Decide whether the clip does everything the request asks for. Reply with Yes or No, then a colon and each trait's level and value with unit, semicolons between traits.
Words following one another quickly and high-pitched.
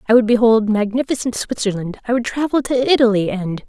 No: average, 180 wpm; high, 230 Hz